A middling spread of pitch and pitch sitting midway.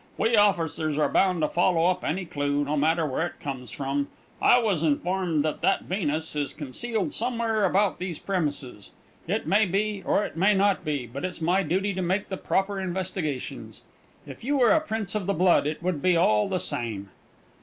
Yes: average, 4.8 semitones; medium, 180 Hz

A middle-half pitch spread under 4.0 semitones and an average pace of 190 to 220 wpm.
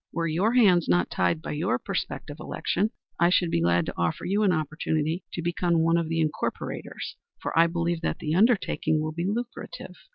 Yes: narrow, 2.5 semitones; average, 195 wpm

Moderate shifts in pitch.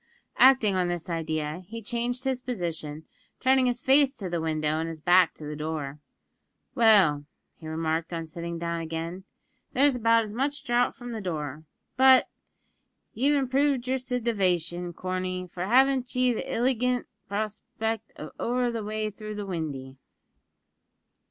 No: wide, 7.0 semitones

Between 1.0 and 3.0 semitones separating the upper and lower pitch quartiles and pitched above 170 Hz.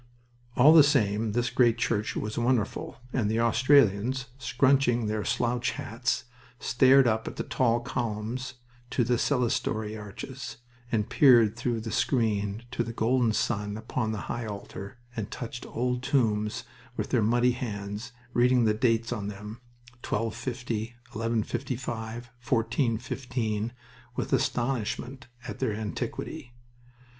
No: narrow, 2.5 semitones; low, 115 Hz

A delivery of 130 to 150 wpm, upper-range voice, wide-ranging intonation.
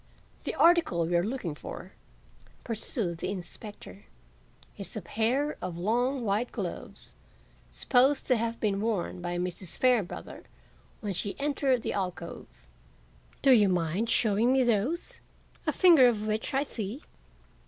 Yes: average, 140 wpm; high, 220 Hz; wide, 5.7 semitones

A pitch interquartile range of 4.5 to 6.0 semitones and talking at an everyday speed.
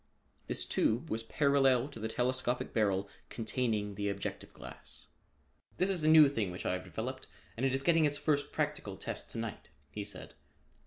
Yes: average, 5.3 semitones; average, 180 wpm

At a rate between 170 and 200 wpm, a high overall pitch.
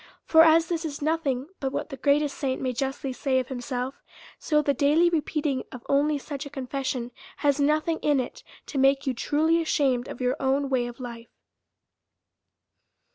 Yes: average, 180 wpm; very high, 275 Hz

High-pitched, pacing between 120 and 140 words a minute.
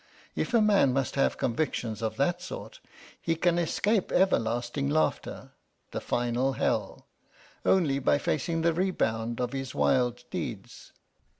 No: medium, 140 Hz; slow, 135 wpm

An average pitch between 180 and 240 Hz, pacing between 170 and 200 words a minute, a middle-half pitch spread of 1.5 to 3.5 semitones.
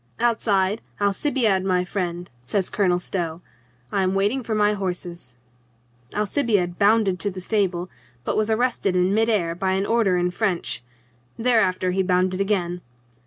No: high, 190 Hz; average, 150 wpm; average, 2.9 semitones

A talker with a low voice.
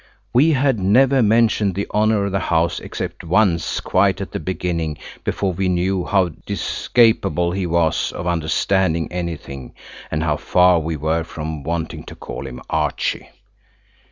Yes: very low, 90 Hz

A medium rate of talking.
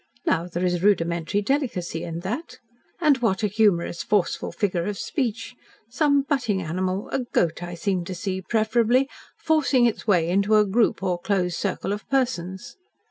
Yes: average, 165 wpm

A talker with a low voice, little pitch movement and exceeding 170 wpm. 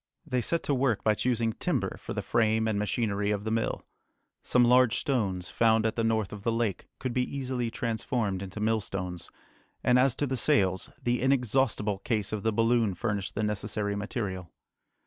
No: low, 110 Hz; average, 3.0 semitones; average, 185 wpm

